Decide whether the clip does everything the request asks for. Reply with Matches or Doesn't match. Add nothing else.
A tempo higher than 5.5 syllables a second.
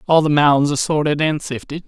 Matches